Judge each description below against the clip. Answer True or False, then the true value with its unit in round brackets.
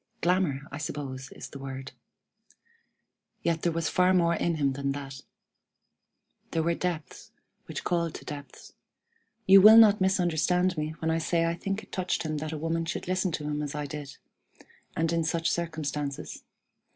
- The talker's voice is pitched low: False (160 Hz)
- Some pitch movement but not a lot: True (3.1 semitones)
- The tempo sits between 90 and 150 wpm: False (175 wpm)